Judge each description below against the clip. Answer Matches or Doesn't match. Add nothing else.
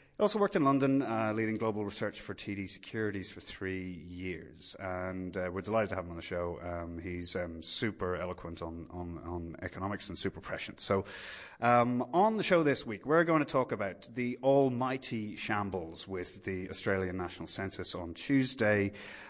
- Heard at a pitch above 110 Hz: Doesn't match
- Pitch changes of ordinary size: Matches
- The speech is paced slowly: Doesn't match